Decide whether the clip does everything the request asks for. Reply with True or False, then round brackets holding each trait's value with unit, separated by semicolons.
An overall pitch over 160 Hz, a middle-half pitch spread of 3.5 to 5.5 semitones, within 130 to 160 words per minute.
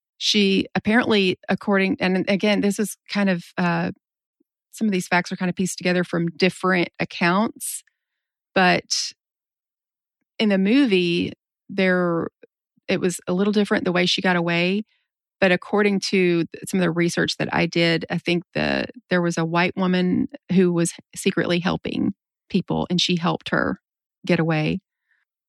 False (185 Hz; 2.9 semitones; 155 wpm)